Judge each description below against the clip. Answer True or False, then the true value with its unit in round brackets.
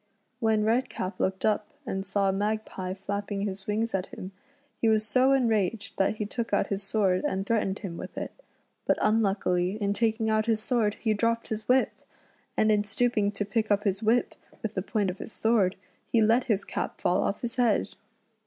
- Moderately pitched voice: False (210 Hz)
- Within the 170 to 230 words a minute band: True (195 wpm)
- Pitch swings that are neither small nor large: False (2.2 semitones)